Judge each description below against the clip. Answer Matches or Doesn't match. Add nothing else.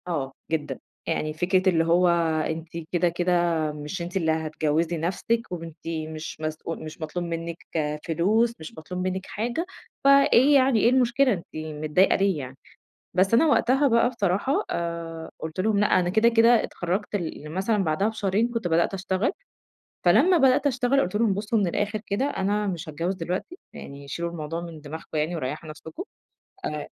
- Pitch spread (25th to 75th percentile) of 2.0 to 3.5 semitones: Doesn't match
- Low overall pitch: Doesn't match